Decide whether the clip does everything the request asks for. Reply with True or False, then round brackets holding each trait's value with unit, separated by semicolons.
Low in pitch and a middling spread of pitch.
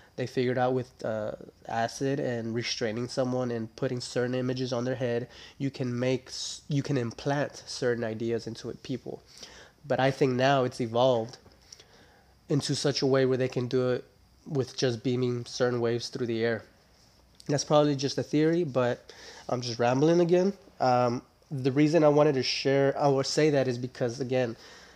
False (130 Hz; 2.2 semitones)